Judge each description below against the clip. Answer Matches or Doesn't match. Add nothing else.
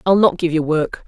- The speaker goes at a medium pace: Doesn't match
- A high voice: Doesn't match